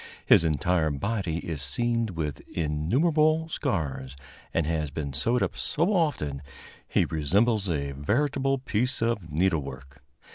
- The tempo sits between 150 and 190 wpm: No, slow, 135 wpm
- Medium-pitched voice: No, very low, 85 Hz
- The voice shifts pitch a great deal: Yes, wide, 8.5 semitones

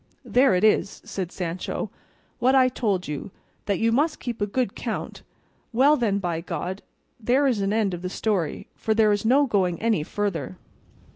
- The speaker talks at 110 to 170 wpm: No, average, 185 wpm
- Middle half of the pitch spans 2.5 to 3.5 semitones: No, average, 4.7 semitones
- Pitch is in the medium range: No, high, 210 Hz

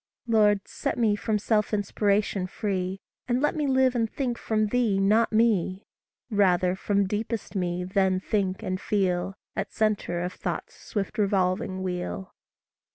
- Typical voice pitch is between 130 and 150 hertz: No, high, 200 Hz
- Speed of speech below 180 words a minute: Yes, average, 150 wpm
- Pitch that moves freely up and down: No, average, 2.7 semitones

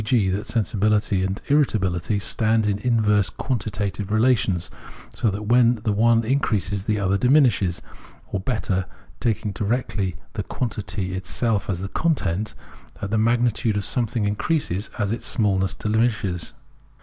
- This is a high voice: No, low, 105 Hz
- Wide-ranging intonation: No, average, 3.0 semitones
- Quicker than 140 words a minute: No, slow, 135 wpm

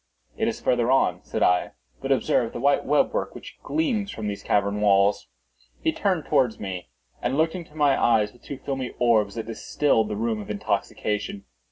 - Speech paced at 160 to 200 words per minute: Yes, average, 190 wpm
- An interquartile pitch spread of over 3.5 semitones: Yes, average, 5.1 semitones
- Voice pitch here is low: Yes, low, 115 Hz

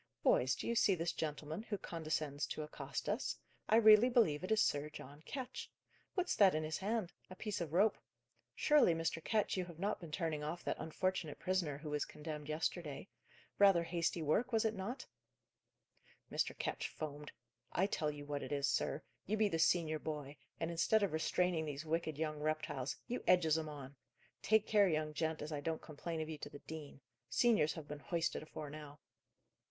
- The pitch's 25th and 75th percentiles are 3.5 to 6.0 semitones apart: Yes, average, 3.9 semitones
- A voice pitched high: No, medium, 160 Hz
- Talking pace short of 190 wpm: No, average, 195 wpm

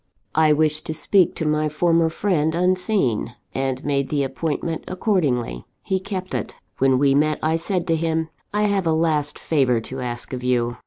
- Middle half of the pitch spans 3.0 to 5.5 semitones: Yes, average, 4.2 semitones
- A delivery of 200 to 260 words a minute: No, average, 180 wpm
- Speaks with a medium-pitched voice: Yes, medium, 155 Hz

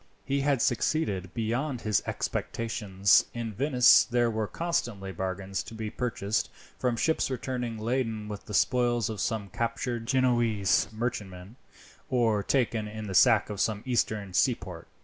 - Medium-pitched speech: No, low, 115 Hz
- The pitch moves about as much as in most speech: Yes, average, 3.3 semitones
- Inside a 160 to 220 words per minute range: No, average, 145 wpm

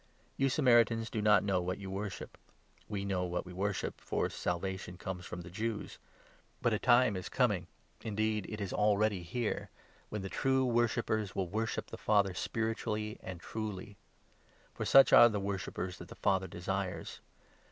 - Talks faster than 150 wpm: Yes, average, 175 wpm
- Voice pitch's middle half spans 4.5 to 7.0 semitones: No, average, 3.0 semitones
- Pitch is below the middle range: Yes, low, 105 Hz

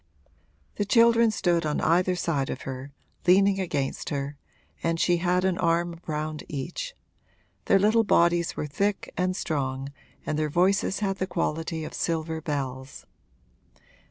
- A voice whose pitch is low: No, medium, 170 Hz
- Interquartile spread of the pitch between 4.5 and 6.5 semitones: No, average, 4.0 semitones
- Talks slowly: No, average, 145 wpm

